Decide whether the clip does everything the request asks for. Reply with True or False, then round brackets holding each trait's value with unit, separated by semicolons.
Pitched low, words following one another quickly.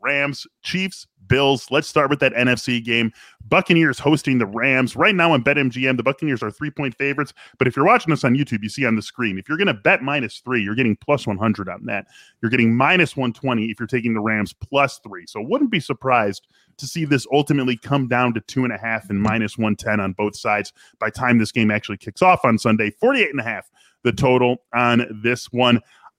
True (125 Hz; 220 wpm)